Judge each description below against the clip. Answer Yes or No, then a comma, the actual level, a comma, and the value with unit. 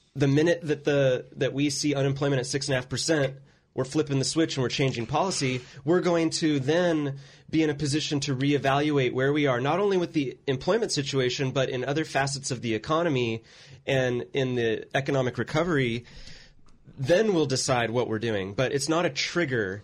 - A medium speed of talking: Yes, average, 180 wpm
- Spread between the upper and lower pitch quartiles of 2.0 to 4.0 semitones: Yes, average, 3.0 semitones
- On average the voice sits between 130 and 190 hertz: Yes, medium, 140 Hz